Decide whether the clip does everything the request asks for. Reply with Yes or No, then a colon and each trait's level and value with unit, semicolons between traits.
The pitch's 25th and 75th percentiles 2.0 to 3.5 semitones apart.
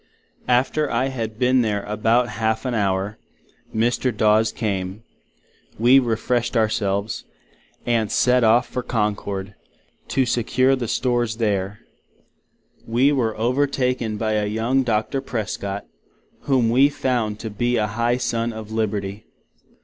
Yes: average, 2.7 semitones